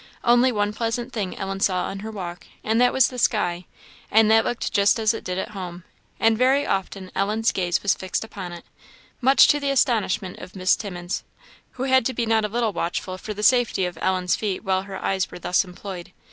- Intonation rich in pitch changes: No, average, 3.7 semitones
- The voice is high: Yes, high, 205 Hz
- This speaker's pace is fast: Yes, fast, 215 wpm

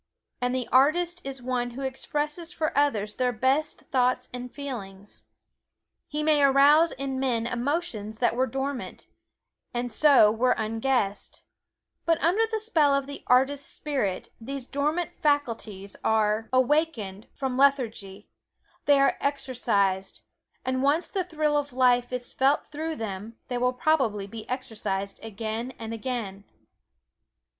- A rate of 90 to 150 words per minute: Yes, slow, 135 wpm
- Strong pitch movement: No, average, 4.3 semitones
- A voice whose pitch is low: No, very high, 255 Hz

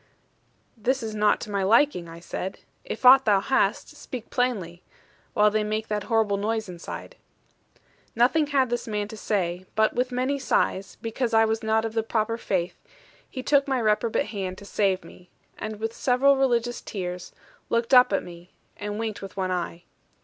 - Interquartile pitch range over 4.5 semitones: No, average, 3.7 semitones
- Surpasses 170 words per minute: Yes, average, 180 wpm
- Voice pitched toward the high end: Yes, high, 220 Hz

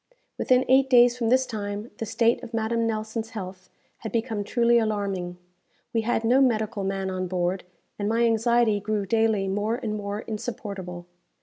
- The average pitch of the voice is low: No, high, 220 Hz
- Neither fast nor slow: Yes, average, 170 wpm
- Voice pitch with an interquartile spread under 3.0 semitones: Yes, narrow, 2.5 semitones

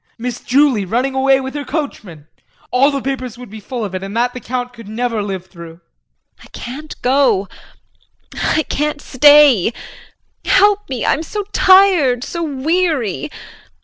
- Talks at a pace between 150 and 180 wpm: Yes, average, 160 wpm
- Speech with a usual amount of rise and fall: Yes, average, 4.6 semitones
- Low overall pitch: No, very high, 255 Hz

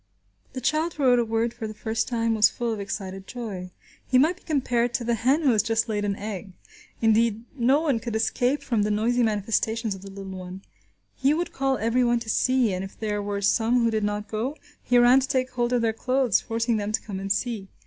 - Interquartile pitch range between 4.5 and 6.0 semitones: No, average, 3.2 semitones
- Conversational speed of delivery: No, fast, 235 wpm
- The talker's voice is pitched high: Yes, high, 230 Hz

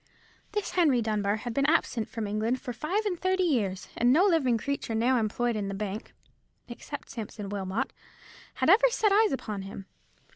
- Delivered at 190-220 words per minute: No, average, 180 wpm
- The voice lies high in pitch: Yes, high, 240 Hz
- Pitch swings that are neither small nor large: No, wide, 7.3 semitones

